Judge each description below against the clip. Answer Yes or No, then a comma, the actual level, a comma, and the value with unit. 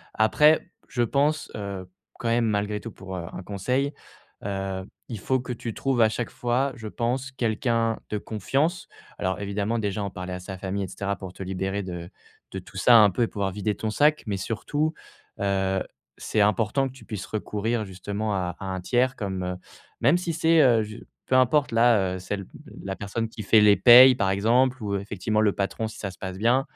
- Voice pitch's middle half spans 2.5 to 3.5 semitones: No, average, 3.9 semitones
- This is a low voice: Yes, low, 105 Hz